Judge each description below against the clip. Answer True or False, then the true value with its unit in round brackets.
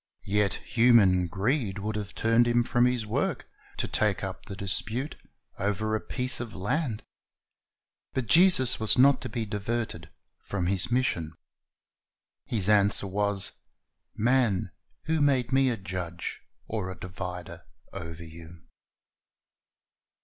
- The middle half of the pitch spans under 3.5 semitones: False (4.4 semitones)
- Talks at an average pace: False (130 wpm)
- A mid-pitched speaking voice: False (105 Hz)